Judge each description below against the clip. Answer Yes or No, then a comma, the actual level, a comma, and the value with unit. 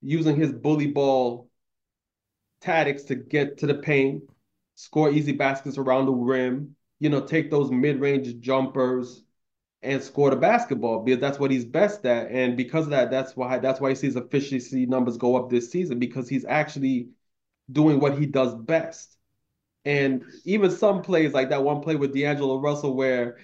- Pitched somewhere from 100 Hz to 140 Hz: Yes, low, 135 Hz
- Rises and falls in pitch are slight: Yes, narrow, 2.3 semitones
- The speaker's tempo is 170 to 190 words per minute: Yes, average, 175 wpm